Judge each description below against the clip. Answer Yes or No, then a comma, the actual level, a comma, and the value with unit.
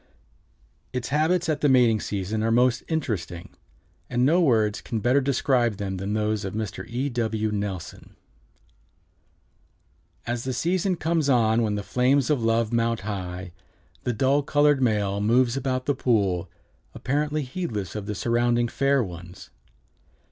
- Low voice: Yes, low, 120 Hz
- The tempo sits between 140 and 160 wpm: Yes, average, 150 wpm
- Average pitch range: Yes, average, 4.5 semitones